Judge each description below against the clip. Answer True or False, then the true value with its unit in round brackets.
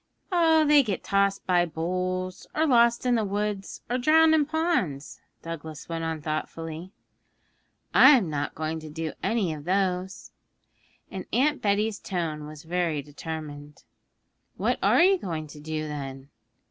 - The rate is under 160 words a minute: True (140 wpm)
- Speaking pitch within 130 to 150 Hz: False (180 Hz)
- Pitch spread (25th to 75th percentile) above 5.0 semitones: True (5.6 semitones)